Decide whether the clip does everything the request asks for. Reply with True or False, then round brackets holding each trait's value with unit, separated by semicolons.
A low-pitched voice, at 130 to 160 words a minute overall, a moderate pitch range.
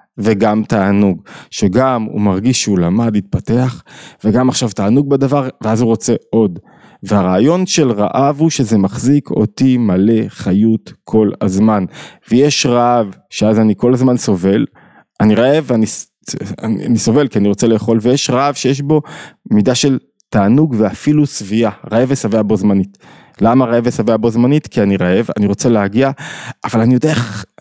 True (115 Hz; 150 wpm; 3.7 semitones)